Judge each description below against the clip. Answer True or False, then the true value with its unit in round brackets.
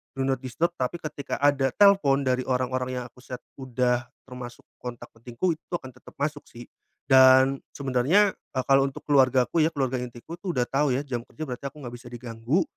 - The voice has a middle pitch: False (130 Hz)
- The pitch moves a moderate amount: False (2.3 semitones)